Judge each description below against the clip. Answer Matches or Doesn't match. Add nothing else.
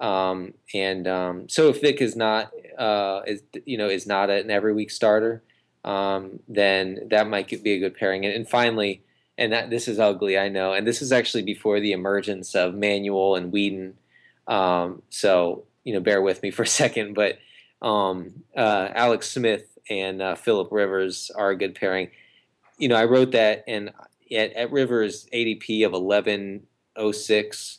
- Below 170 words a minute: Doesn't match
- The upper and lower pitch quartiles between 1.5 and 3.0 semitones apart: Matches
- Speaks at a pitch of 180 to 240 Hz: Doesn't match